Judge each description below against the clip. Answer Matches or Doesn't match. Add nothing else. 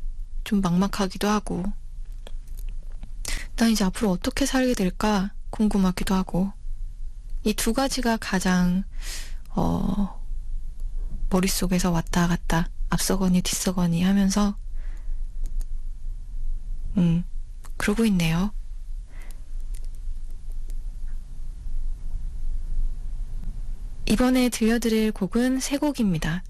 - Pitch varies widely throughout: Doesn't match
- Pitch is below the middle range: Doesn't match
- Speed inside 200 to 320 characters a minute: Doesn't match